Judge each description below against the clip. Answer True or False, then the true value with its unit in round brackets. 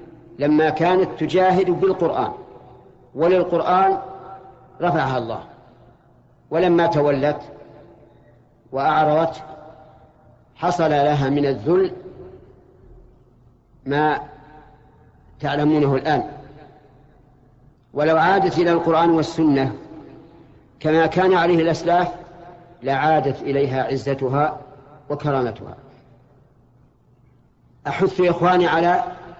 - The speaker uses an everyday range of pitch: True (4.1 semitones)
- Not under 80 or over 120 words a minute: False (65 wpm)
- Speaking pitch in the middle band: True (150 Hz)